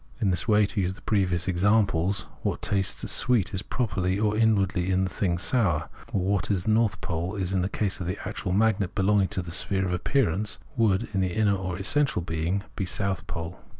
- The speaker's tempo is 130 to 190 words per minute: No, fast, 205 wpm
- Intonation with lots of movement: No, narrow, 2.5 semitones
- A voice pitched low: Yes, very low, 95 Hz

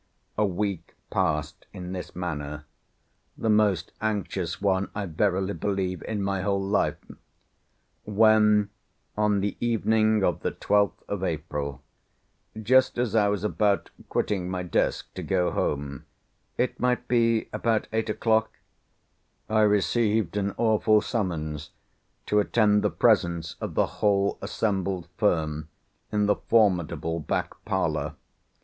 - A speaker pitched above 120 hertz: No, low, 100 Hz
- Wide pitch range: No, average, 3.2 semitones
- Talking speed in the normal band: No, slow, 130 wpm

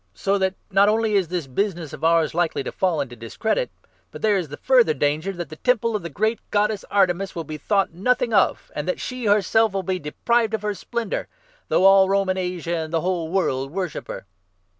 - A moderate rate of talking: No, fast, 225 wpm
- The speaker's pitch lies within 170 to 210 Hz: Yes, high, 190 Hz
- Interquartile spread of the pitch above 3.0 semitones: Yes, average, 4.3 semitones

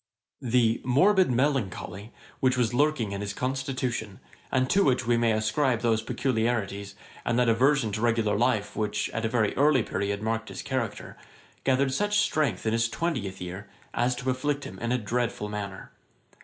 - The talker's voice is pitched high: No, low, 115 Hz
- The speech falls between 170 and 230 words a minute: Yes, average, 175 wpm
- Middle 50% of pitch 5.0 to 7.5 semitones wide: No, average, 3.5 semitones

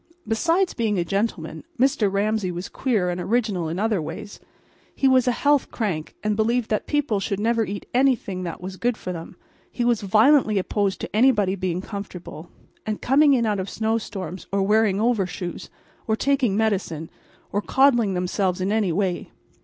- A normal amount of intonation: Yes, average, 4.0 semitones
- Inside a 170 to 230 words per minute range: Yes, average, 175 wpm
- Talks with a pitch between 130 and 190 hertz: No, high, 210 Hz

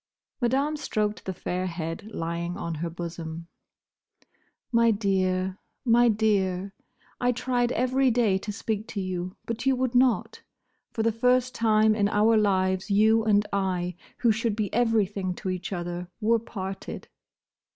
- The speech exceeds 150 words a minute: No, average, 145 wpm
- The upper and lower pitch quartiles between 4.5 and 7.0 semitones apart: No, average, 3.8 semitones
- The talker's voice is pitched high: Yes, high, 210 Hz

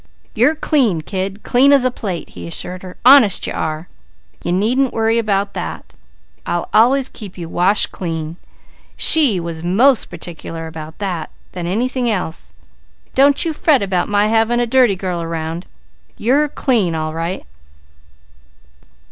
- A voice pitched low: No, high, 200 Hz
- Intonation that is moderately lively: No, wide, 6.4 semitones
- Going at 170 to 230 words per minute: No, average, 150 wpm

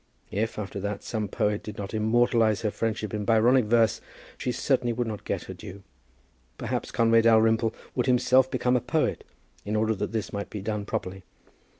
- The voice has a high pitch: No, low, 110 Hz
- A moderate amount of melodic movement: No, narrow, 2.1 semitones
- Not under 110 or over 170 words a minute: No, average, 185 wpm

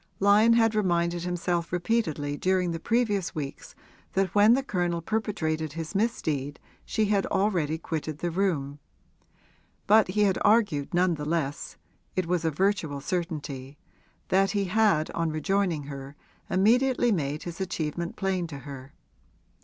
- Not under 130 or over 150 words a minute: Yes, average, 145 wpm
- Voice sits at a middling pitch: Yes, medium, 175 Hz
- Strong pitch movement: No, average, 4.7 semitones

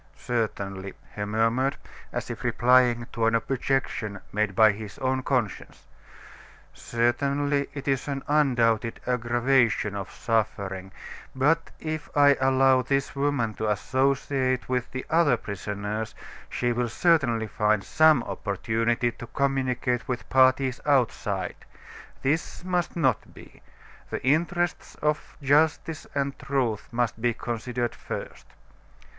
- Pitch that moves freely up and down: No, average, 3.5 semitones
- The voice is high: No, low, 125 Hz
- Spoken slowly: Yes, slow, 120 wpm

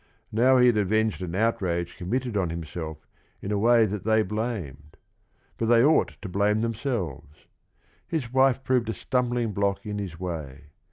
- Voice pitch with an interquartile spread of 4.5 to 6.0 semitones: Yes, average, 5.1 semitones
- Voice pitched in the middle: No, low, 105 Hz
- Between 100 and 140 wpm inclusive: No, average, 165 wpm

